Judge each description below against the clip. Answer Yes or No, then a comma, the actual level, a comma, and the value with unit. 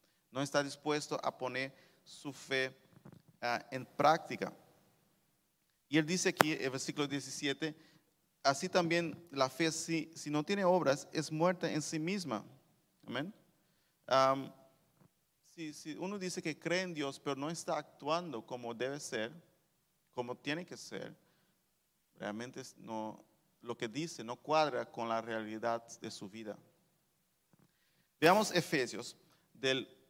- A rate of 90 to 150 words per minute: Yes, average, 135 wpm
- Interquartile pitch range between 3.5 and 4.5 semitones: Yes, average, 4.2 semitones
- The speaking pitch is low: No, medium, 150 Hz